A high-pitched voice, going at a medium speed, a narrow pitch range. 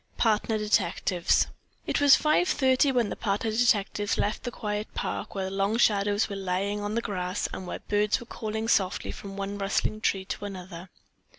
Yes: high, 205 Hz; average, 180 wpm; narrow, 2.2 semitones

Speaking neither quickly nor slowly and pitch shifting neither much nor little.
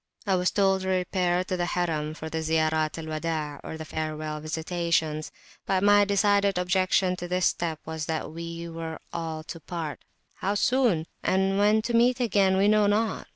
Yes: average, 175 wpm; average, 3.5 semitones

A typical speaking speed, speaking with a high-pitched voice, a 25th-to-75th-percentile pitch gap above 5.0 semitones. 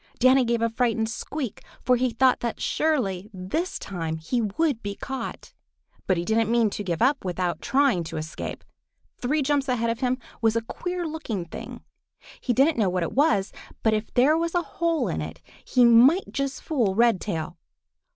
Yes: average, 185 wpm; high, 235 Hz; wide, 5.5 semitones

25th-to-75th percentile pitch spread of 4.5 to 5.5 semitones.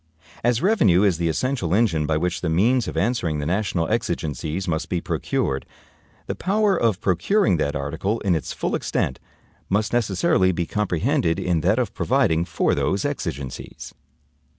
Yes: average, 5.2 semitones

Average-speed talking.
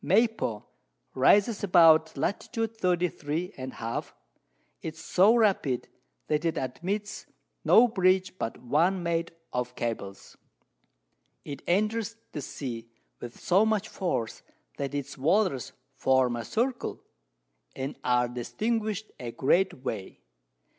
No: slow, 120 wpm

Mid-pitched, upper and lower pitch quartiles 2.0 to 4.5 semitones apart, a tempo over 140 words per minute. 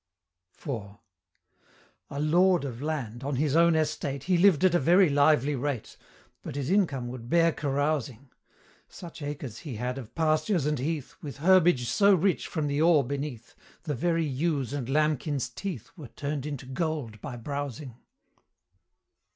Yes: medium, 145 Hz; average, 3.6 semitones; average, 155 wpm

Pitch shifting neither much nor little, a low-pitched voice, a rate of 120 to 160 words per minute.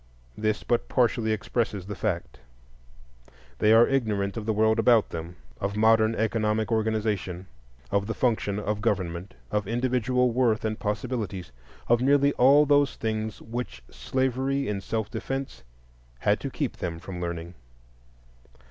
Yes: average, 3.3 semitones; low, 110 Hz; average, 140 wpm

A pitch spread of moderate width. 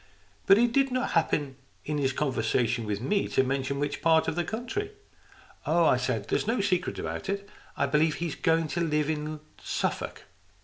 No: wide, 6.1 semitones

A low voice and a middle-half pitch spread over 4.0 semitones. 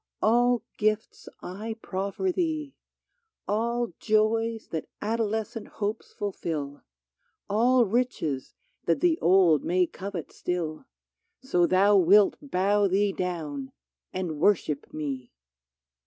No: high, 205 Hz; average, 4.6 semitones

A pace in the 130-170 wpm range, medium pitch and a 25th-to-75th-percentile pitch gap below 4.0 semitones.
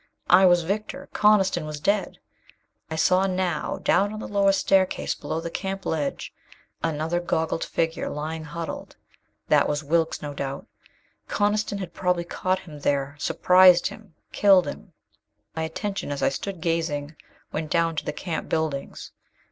Yes: average, 155 wpm; medium, 170 Hz; average, 3.4 semitones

